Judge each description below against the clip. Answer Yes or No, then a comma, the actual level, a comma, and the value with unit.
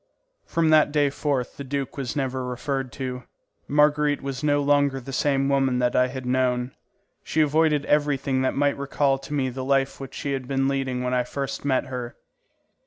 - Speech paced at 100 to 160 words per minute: No, average, 190 wpm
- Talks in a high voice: No, low, 135 Hz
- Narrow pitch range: Yes, narrow, 1.8 semitones